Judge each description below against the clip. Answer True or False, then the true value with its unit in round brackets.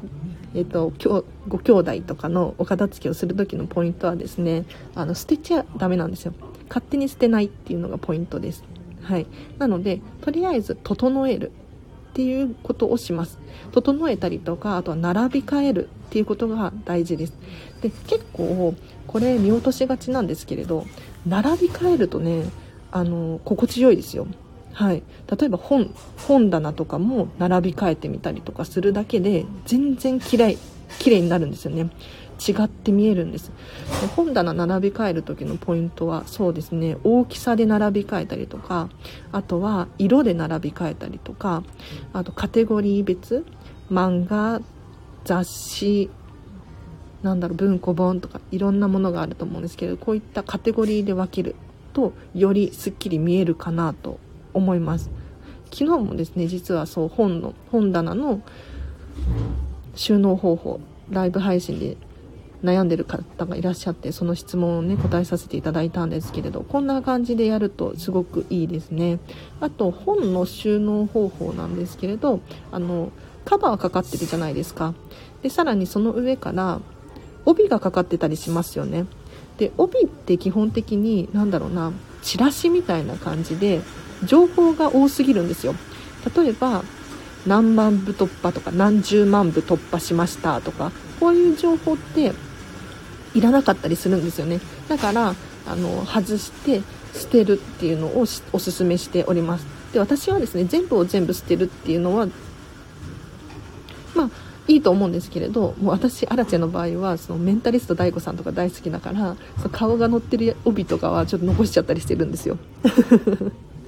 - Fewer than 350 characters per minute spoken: True (330 characters per minute)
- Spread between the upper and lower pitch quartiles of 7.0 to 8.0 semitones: False (5.1 semitones)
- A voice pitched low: False (190 Hz)